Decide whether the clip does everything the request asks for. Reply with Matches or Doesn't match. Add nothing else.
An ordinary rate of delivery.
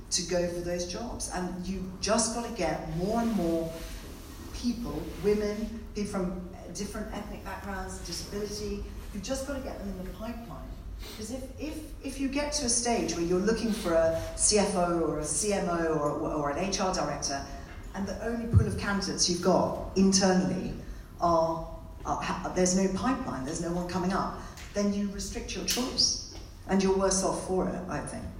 Matches